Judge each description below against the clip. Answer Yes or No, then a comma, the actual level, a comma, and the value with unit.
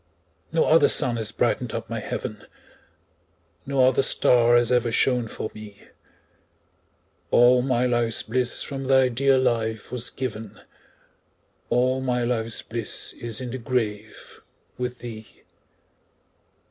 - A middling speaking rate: No, slow, 130 wpm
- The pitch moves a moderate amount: No, narrow, 2.1 semitones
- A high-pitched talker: No, low, 120 Hz